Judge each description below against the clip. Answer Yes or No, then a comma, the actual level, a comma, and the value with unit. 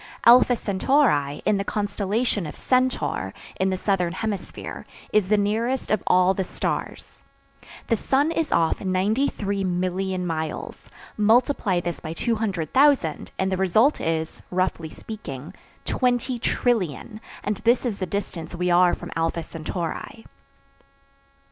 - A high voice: Yes, high, 195 Hz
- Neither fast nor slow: No, slow, 125 wpm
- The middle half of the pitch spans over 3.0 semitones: Yes, average, 4.8 semitones